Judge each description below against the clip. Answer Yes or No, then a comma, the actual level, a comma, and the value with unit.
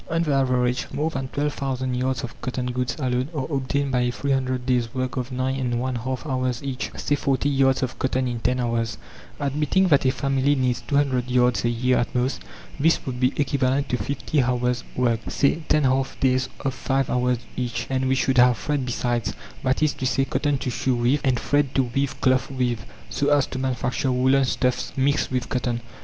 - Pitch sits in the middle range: No, low, 130 Hz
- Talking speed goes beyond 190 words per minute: Yes, fast, 205 wpm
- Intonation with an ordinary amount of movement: No, narrow, 1.6 semitones